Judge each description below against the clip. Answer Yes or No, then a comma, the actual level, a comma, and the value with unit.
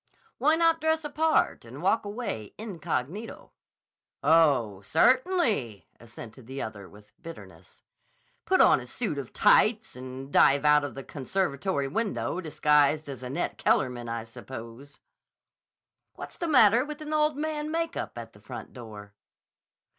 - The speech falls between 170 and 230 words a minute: No, average, 140 wpm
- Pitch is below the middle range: No, medium, 150 Hz